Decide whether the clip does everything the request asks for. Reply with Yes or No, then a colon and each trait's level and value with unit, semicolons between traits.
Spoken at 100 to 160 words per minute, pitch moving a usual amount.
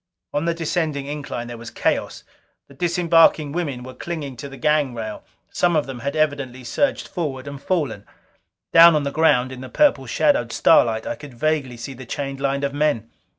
No: average, 195 wpm; average, 3.3 semitones